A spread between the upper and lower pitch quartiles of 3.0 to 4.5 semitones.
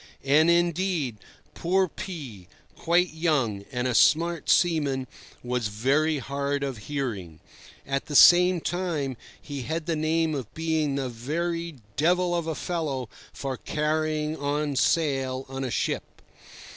Yes: average, 3.8 semitones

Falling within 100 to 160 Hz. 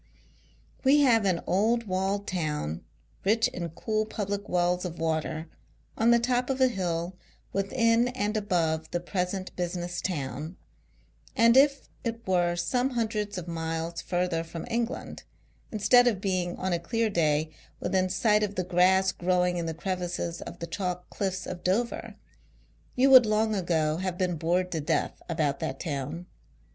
No: medium, 185 Hz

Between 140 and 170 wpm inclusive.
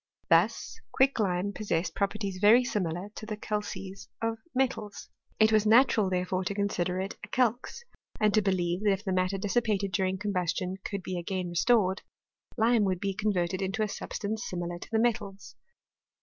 No: average, 180 wpm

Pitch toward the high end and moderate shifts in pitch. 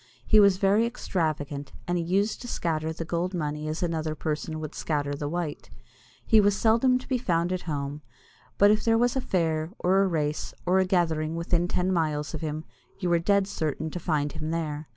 No: medium, 170 Hz; average, 3.7 semitones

